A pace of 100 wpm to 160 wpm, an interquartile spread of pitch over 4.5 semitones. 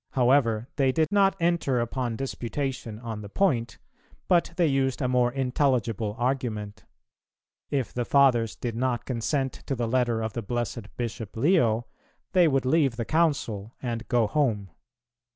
No: average, 150 wpm; average, 3.2 semitones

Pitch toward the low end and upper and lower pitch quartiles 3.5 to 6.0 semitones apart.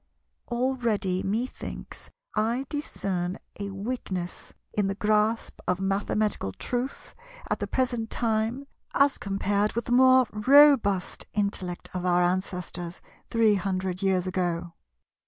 No: high, 205 Hz; average, 4.3 semitones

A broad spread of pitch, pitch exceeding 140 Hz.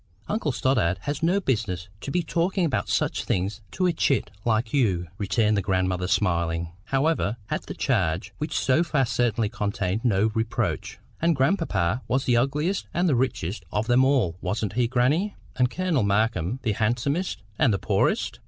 No: wide, 6.1 semitones; low, 120 Hz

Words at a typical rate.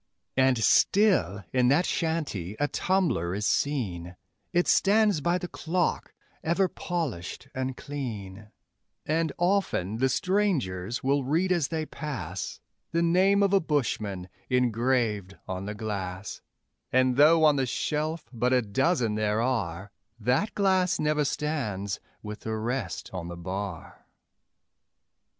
No: slow, 130 wpm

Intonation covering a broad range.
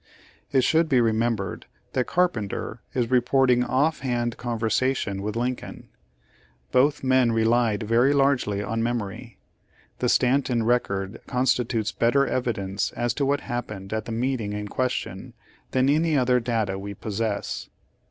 No: average, 2.9 semitones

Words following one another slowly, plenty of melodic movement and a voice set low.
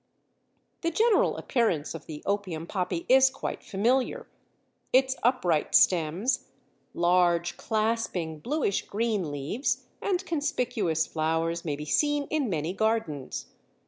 No: slow, 115 wpm; wide, 7.7 semitones; high, 200 Hz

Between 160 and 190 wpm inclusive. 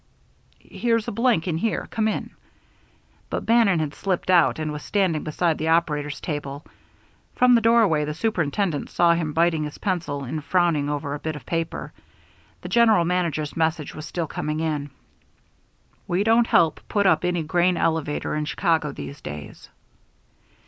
Yes: average, 165 wpm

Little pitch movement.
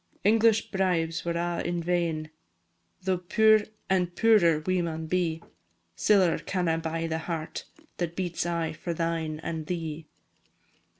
Yes: narrow, 2.0 semitones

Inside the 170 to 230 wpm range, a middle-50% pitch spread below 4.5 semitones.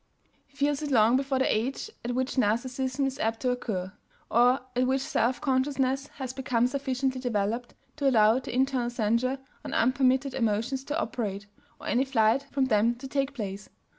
Yes: average, 175 wpm; narrow, 2.6 semitones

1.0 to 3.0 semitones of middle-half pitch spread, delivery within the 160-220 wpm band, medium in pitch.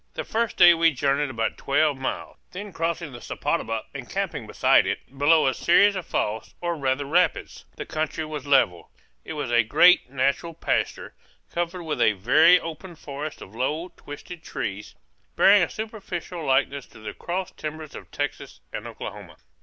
No: average, 4.5 semitones; average, 170 wpm; medium, 155 Hz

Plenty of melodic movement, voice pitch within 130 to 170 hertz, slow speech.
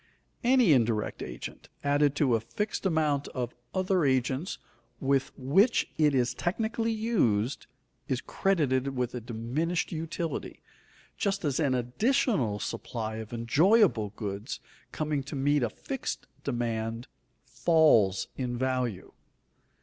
Yes: wide, 5.8 semitones; low, 135 Hz; slow, 120 wpm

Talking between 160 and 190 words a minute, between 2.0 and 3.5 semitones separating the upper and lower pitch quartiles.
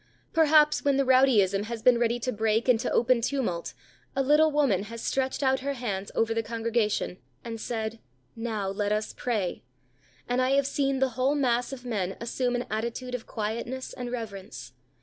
Yes: average, 180 wpm; average, 3.2 semitones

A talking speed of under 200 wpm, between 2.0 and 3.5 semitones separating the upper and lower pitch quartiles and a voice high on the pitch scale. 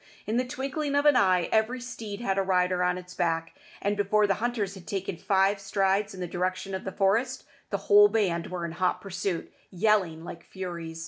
No: fast, 205 wpm; average, 2.8 semitones; high, 195 Hz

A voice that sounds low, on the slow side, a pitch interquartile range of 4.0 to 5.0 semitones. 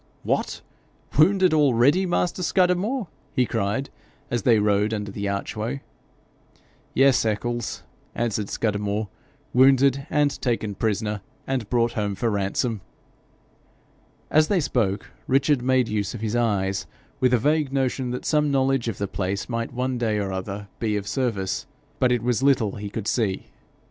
No: low, 120 Hz; average, 155 wpm; average, 4.5 semitones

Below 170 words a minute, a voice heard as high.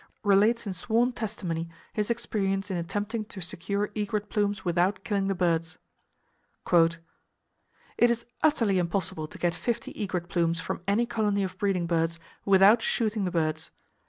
Yes: average, 150 wpm; high, 195 Hz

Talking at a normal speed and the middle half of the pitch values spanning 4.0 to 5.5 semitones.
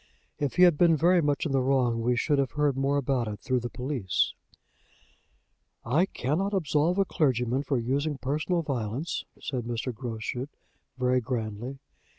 No: average, 165 wpm; average, 3.5 semitones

